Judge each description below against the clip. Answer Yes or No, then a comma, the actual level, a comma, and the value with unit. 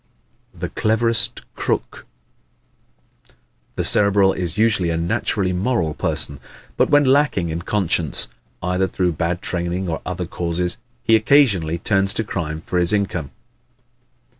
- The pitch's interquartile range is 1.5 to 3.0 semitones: No, average, 4.0 semitones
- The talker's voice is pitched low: Yes, very low, 90 Hz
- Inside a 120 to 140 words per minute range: Yes, slow, 135 wpm